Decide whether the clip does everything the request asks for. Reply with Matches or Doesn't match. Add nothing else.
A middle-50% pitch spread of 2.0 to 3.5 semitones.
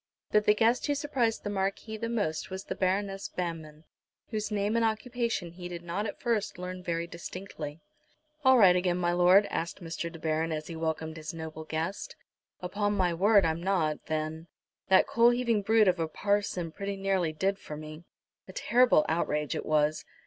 Doesn't match